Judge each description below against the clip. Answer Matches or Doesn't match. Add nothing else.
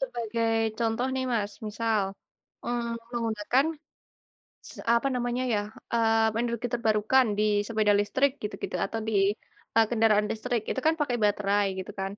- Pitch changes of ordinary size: Doesn't match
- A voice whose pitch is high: Matches